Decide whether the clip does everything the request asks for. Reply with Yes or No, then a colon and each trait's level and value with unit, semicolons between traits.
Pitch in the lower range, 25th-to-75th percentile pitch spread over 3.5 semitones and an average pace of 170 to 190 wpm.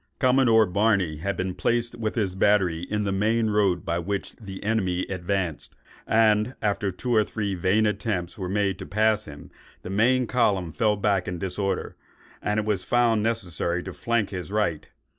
No: low, 100 Hz; average, 3.0 semitones; average, 180 wpm